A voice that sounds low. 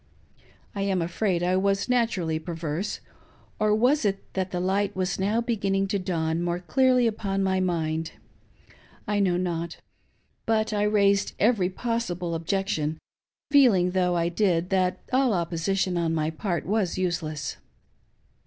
No: medium, 185 Hz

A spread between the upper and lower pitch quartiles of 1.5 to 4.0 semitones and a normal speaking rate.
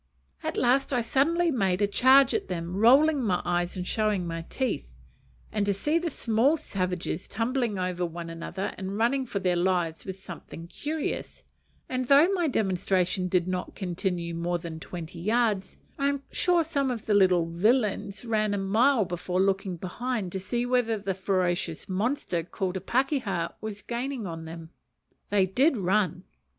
No: wide, 5.5 semitones; average, 170 wpm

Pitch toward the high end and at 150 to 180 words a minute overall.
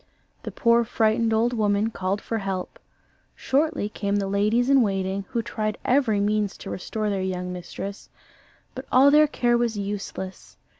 Yes: high, 215 Hz; average, 160 wpm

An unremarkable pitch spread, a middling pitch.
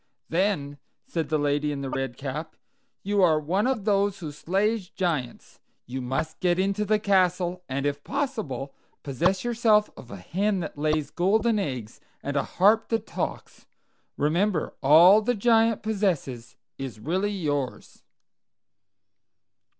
No: wide, 6.2 semitones; medium, 175 Hz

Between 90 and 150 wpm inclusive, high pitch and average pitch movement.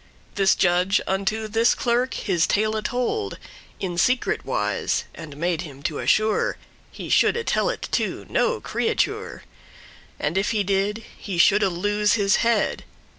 Yes: average, 145 wpm; high, 205 Hz; average, 3.8 semitones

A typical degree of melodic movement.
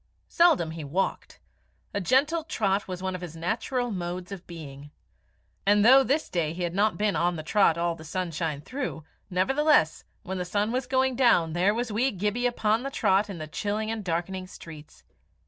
No: wide, 5.7 semitones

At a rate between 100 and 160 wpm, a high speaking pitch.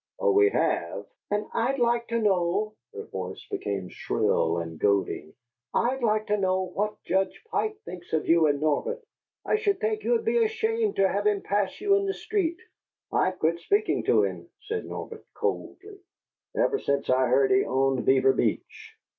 No: average, 175 wpm; high, 210 Hz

